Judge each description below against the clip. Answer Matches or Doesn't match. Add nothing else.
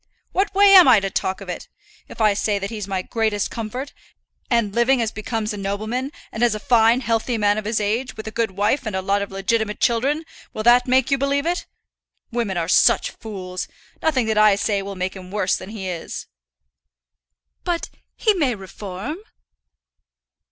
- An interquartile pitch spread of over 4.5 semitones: Doesn't match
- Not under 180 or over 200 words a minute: Matches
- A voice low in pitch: Doesn't match